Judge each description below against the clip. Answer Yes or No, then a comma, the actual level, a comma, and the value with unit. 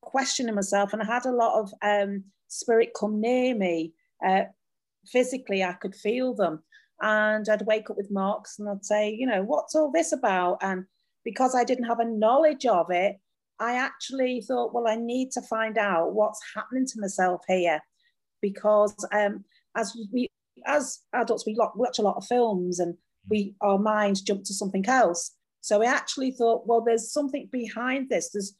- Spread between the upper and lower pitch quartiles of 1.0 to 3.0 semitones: No, average, 3.7 semitones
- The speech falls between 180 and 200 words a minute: Yes, average, 185 wpm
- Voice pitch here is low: No, high, 220 Hz